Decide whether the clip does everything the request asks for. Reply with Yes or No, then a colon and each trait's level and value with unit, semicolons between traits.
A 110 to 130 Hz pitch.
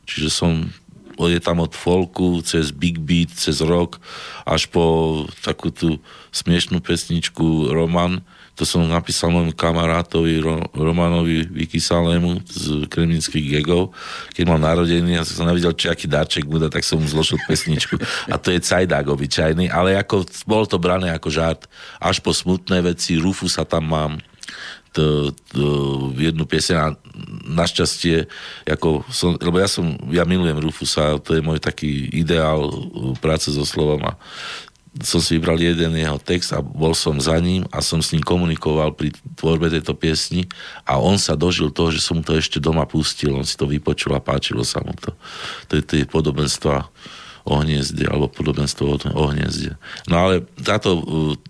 No: very low, 80 Hz